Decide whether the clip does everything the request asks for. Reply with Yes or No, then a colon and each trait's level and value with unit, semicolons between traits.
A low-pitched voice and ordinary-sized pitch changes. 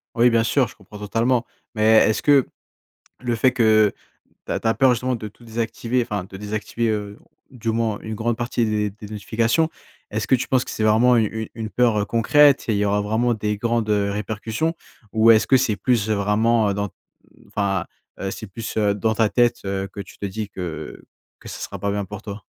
No: low, 110 Hz; narrow, 2.3 semitones